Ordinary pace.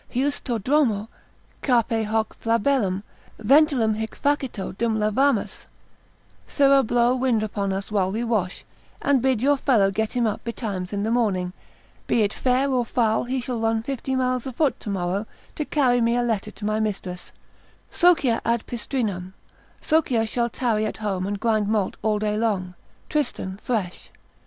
Yes: average, 160 wpm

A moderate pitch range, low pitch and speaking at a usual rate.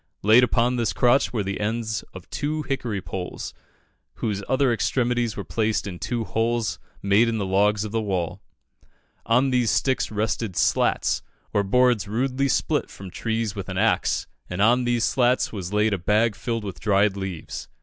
Yes: average, 3.3 semitones; low, 110 Hz; average, 175 wpm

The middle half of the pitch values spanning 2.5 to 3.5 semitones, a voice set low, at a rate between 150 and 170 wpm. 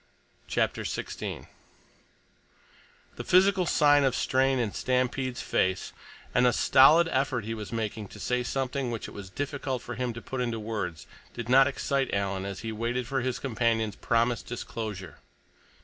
Yes: average, 3.2 semitones; low, 125 Hz; average, 160 wpm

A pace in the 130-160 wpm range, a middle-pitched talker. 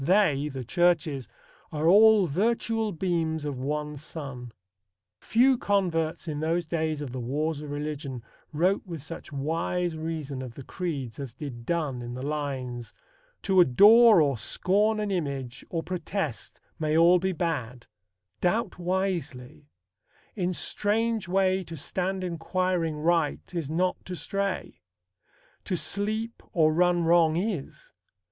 Yes: average, 140 wpm; medium, 165 Hz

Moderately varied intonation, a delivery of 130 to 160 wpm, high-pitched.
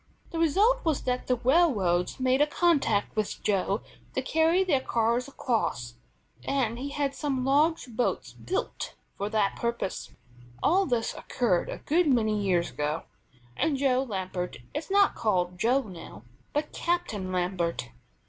No: wide, 7.0 semitones; average, 150 wpm; very high, 250 Hz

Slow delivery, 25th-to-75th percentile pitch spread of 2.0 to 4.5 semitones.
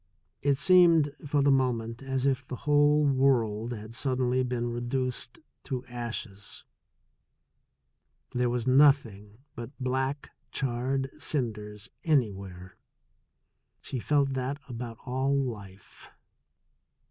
Yes: slow, 115 wpm; average, 2.9 semitones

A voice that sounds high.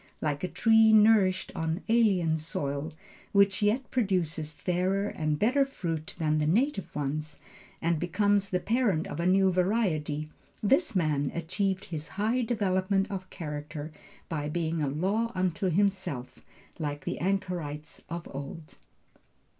No: medium, 180 Hz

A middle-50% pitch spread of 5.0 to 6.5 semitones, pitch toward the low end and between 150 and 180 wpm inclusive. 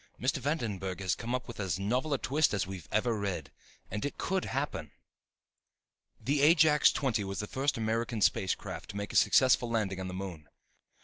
No: wide, 5.4 semitones; low, 110 Hz; average, 190 wpm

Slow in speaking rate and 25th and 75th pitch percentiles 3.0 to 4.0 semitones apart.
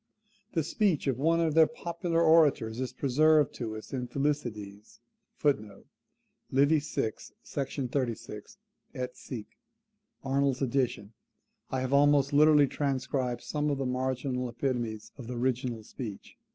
Yes: slow, 130 wpm; average, 3.4 semitones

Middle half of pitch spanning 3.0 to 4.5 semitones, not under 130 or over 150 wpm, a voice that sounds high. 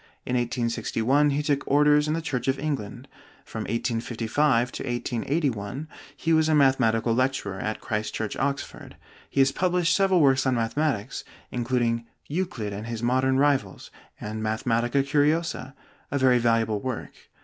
No: average, 4.1 semitones; average, 145 wpm; low, 130 Hz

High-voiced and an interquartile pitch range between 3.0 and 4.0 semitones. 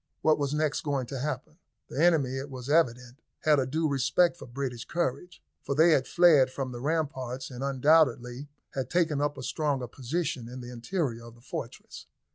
No: medium, 140 Hz; average, 3.6 semitones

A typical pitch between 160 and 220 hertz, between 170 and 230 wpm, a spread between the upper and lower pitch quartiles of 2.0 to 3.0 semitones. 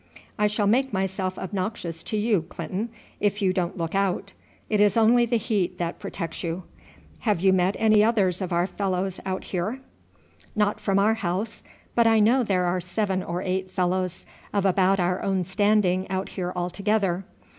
Yes: high, 190 Hz; average, 175 wpm; narrow, 2.5 semitones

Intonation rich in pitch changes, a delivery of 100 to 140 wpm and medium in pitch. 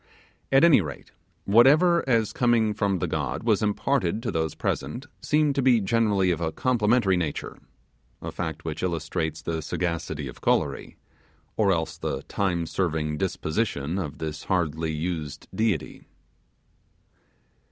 No: wide, 6.1 semitones; slow, 135 wpm; very low, 90 Hz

